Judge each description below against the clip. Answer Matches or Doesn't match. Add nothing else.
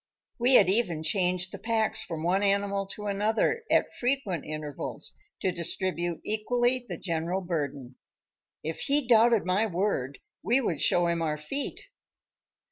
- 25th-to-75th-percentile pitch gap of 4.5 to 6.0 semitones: Matches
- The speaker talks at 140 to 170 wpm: Matches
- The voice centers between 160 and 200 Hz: Matches